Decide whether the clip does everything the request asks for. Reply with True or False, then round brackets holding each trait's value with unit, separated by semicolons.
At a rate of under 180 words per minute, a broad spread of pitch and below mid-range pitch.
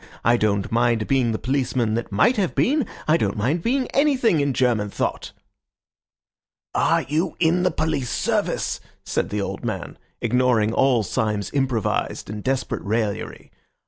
True (150 wpm; 6.4 semitones; 125 Hz)